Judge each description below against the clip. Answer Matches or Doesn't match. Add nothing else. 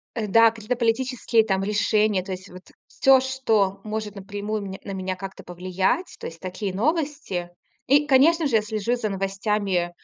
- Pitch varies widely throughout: Doesn't match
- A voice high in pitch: Matches